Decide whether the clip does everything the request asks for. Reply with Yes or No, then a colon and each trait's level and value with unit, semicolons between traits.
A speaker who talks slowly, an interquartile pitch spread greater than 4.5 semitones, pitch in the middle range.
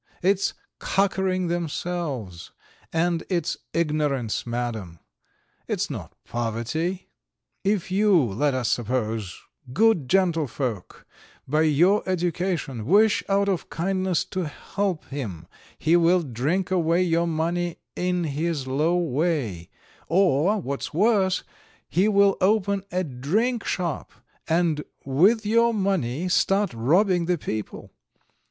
Yes: slow, 110 wpm; wide, 5.5 semitones; medium, 170 Hz